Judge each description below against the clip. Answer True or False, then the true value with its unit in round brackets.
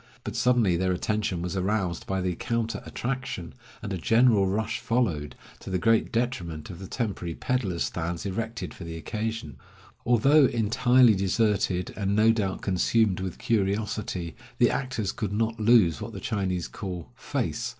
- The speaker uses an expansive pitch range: False (3.8 semitones)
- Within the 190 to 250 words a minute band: False (160 wpm)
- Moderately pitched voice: False (105 Hz)